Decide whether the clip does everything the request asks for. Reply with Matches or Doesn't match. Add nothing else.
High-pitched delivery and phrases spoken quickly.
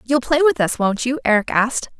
Matches